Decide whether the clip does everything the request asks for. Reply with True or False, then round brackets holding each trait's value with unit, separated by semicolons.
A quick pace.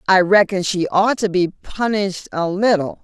False (180 wpm)